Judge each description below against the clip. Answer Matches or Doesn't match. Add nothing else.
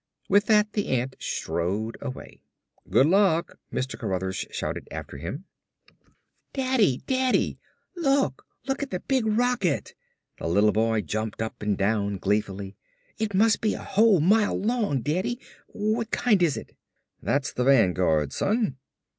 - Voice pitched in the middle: Matches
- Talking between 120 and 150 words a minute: Matches